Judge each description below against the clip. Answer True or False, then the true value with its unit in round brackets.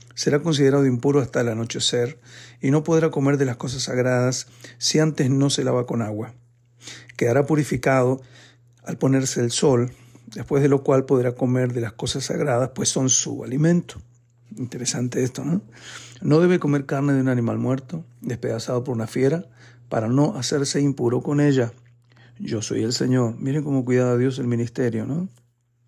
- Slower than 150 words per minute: False (170 wpm)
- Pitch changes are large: False (2.7 semitones)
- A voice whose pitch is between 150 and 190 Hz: False (125 Hz)